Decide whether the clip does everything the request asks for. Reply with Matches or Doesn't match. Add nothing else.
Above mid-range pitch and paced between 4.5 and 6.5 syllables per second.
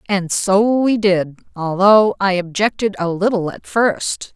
Doesn't match